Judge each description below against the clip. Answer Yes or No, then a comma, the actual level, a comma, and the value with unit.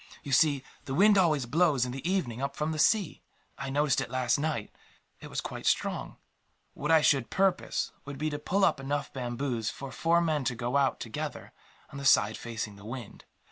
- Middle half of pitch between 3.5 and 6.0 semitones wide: Yes, average, 4.0 semitones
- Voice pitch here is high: No, medium, 140 Hz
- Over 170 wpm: Yes, fast, 205 wpm